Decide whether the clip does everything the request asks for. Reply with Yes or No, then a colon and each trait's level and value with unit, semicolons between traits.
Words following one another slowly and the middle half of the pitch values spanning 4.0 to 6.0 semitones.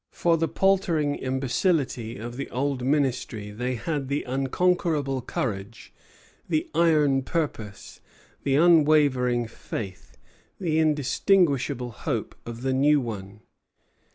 Yes: slow, 110 wpm; average, 4.3 semitones